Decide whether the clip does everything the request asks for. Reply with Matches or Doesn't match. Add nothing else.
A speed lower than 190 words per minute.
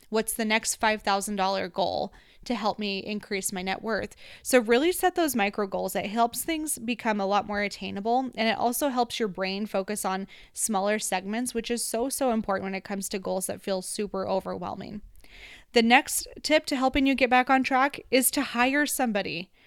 Doesn't match